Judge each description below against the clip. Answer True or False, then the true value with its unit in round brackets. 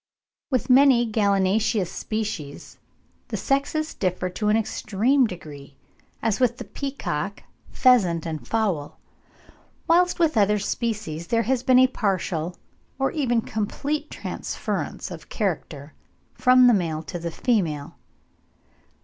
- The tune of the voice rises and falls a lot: True (6.4 semitones)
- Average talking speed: False (125 wpm)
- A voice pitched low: False (215 Hz)